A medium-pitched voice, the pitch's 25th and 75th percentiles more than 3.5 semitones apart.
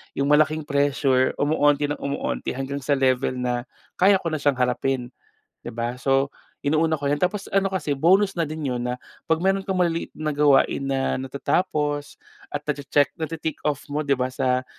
No: medium, 145 Hz; average, 2.8 semitones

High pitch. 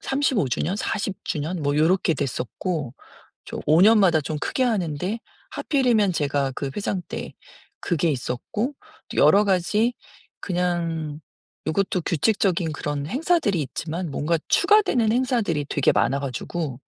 No: medium, 175 Hz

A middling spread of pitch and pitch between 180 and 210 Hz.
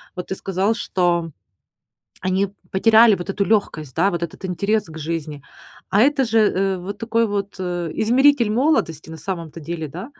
Yes: average, 4.4 semitones; high, 190 Hz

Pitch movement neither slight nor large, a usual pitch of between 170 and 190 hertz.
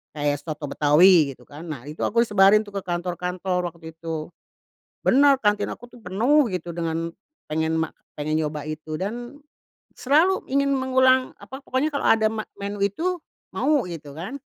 No: wide, 7.4 semitones; medium, 185 Hz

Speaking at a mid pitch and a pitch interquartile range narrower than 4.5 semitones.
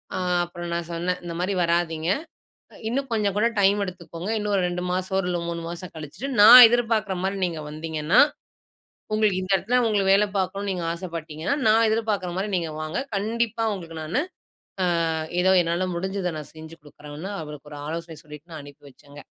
Yes: medium, 180 Hz; average, 3.6 semitones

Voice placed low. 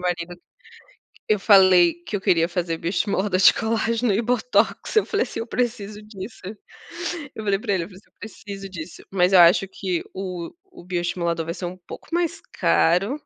No: high, 190 Hz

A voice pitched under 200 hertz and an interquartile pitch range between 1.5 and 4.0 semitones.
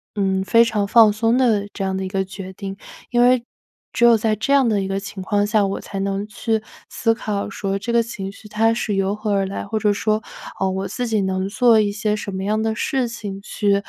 No: high, 210 Hz; narrow, 2.5 semitones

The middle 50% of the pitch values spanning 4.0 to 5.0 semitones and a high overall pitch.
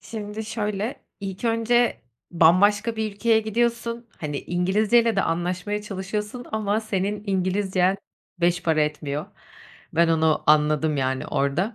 Yes: average, 4.5 semitones; high, 200 Hz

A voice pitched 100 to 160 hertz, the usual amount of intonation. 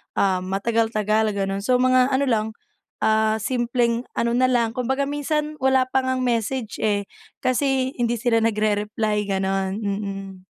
No: high, 230 Hz; average, 3.7 semitones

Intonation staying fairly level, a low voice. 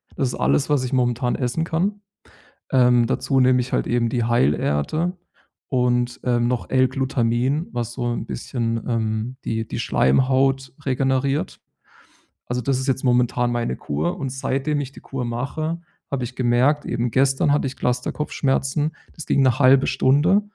Yes: narrow, 2.1 semitones; low, 130 Hz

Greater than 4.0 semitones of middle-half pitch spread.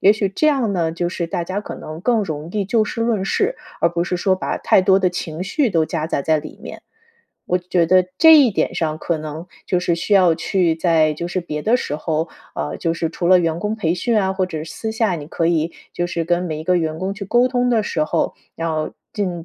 No: average, 3.5 semitones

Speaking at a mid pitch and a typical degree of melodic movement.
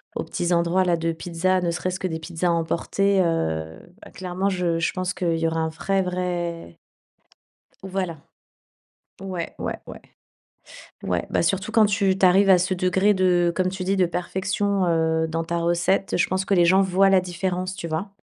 No: medium, 180 Hz; narrow, 2.1 semitones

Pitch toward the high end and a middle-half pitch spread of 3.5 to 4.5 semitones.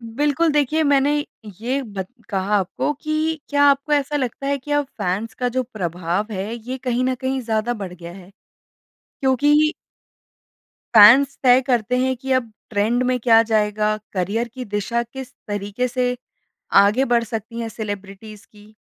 Yes: high, 240 Hz; average, 4.2 semitones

